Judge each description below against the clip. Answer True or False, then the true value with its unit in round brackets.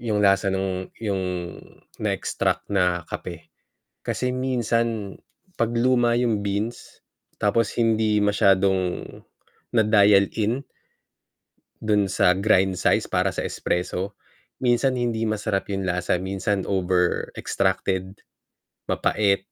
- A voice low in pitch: True (100 Hz)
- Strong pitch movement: False (3.1 semitones)